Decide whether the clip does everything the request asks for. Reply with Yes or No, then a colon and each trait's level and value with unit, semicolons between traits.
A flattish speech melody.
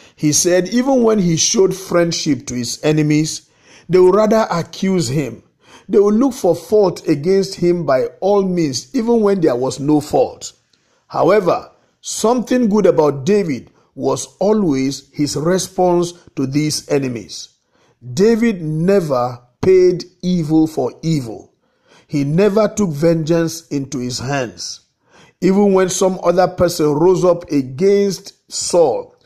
No: average, 4.9 semitones